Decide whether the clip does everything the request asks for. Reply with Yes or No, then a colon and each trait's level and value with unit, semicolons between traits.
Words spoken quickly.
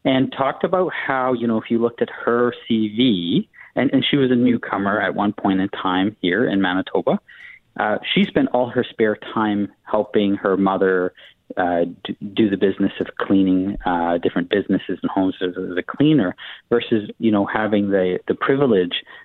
No: average, 180 wpm